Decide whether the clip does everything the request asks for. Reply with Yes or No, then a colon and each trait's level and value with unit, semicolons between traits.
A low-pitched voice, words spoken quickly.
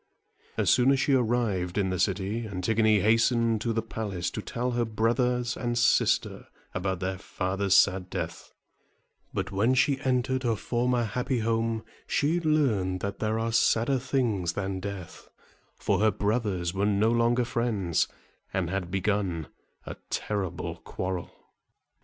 No: low, 110 Hz; average, 145 wpm